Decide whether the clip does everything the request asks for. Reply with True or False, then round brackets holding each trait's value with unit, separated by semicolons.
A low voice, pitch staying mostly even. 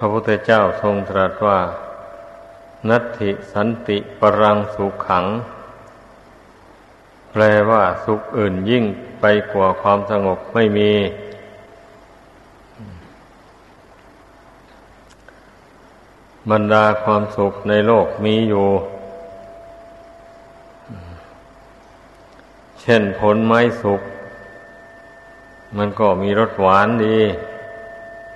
True (105 Hz; 2.0 semitones)